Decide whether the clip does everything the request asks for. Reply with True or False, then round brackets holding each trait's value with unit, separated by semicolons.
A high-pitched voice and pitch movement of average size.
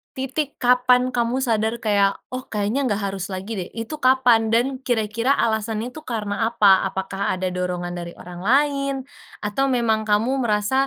True (220 Hz; 3.7 semitones)